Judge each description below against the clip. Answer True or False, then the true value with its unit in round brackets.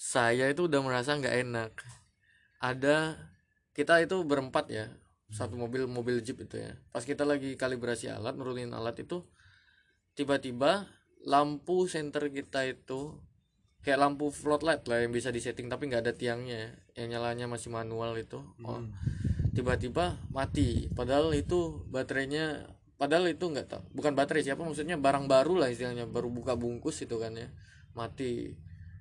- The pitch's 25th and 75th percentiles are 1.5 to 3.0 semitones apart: False (3.5 semitones)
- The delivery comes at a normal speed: False (145 wpm)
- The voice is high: False (125 Hz)